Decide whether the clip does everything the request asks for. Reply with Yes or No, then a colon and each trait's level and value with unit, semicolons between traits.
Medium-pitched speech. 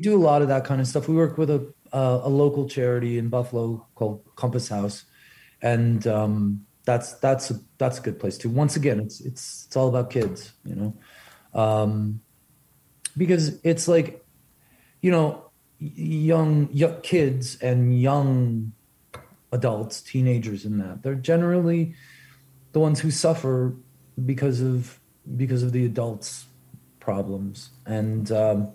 No: low, 130 Hz